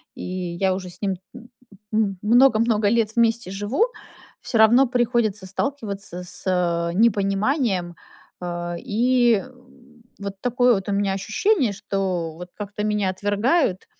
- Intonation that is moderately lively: Yes, average, 3.9 semitones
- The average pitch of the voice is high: Yes, high, 205 Hz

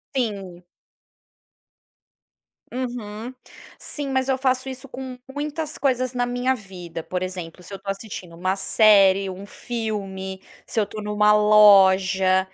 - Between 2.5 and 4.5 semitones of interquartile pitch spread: No, average, 4.9 semitones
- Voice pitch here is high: Yes, high, 210 Hz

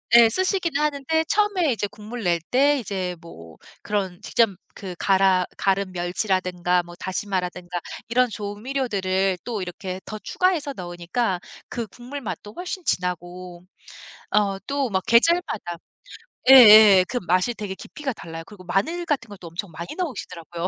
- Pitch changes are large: Yes, wide, 5.8 semitones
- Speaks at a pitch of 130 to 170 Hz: No, high, 200 Hz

